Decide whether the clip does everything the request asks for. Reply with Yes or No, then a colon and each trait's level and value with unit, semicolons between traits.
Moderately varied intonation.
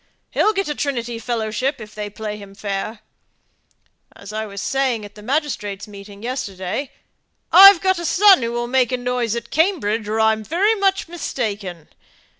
No: wide, 5.7 semitones